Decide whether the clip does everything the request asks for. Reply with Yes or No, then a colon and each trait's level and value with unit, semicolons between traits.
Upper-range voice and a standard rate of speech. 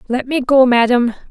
Yes: very high, 250 Hz; average, 185 wpm